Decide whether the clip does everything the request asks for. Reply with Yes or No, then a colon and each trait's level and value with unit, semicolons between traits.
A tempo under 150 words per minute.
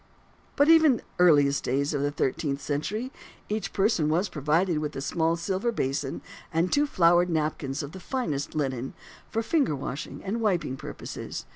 No: average, 170 wpm